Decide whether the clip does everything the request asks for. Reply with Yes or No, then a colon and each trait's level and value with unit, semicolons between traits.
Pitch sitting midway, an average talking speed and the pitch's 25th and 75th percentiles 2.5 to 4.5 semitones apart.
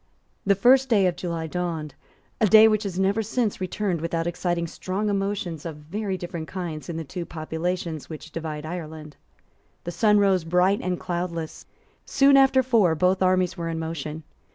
Yes: medium, 180 Hz; average, 170 wpm; average, 3.4 semitones